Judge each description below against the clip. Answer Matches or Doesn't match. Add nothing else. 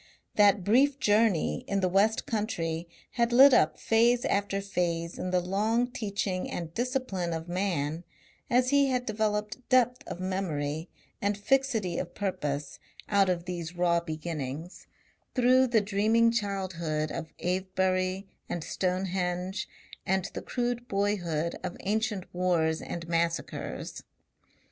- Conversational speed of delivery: Doesn't match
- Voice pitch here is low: Doesn't match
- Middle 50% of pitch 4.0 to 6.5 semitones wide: Matches